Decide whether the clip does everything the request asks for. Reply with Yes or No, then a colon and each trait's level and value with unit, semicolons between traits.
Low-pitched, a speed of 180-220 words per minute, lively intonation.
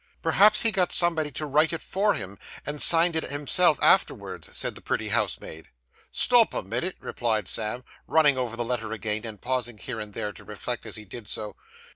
Yes: low, 125 Hz; average, 195 wpm; wide, 7.0 semitones